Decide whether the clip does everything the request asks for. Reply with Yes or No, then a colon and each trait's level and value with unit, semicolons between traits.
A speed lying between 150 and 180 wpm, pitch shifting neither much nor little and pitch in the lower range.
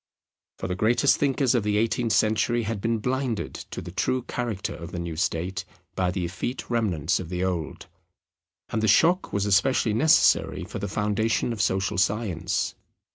Yes: average, 175 wpm; average, 4.2 semitones; low, 105 Hz